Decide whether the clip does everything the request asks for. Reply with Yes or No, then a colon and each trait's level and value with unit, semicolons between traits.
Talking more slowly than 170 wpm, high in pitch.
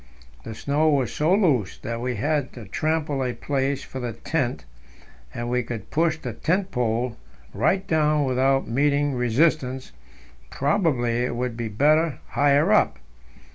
No: average, 150 wpm; low, 135 Hz